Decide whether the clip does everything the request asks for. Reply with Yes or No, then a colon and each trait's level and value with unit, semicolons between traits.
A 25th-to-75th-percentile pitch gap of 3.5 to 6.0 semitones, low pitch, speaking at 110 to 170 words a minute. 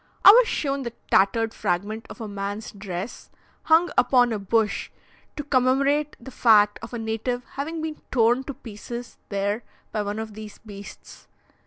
No: average, 4.3 semitones; high, 225 Hz; average, 165 wpm